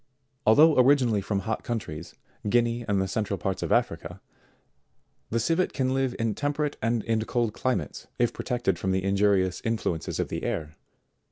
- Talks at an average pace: Yes, average, 165 wpm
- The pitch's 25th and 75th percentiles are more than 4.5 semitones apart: No, average, 4.0 semitones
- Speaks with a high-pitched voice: No, low, 110 Hz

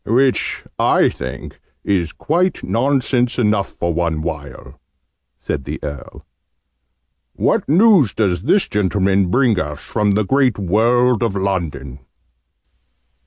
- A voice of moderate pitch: No, low, 105 Hz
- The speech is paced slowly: Yes, slow, 120 wpm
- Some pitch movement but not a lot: No, wide, 6.2 semitones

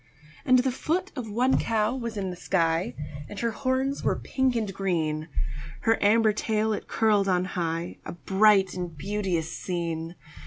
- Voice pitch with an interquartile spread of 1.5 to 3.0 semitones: No, average, 4.6 semitones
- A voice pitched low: No, high, 205 Hz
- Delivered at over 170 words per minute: No, average, 165 wpm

